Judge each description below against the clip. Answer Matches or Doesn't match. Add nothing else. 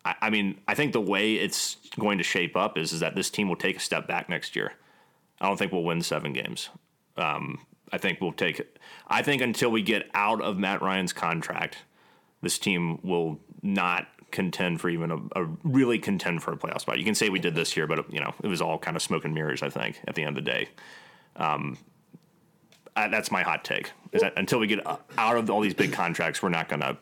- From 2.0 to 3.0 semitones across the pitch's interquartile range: Doesn't match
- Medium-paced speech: Doesn't match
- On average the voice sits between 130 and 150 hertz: Doesn't match